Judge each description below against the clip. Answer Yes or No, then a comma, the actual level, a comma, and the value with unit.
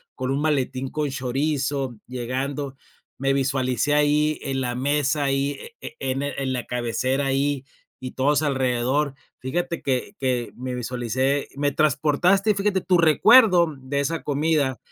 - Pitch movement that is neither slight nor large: No, narrow, 2.3 semitones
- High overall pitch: No, medium, 140 Hz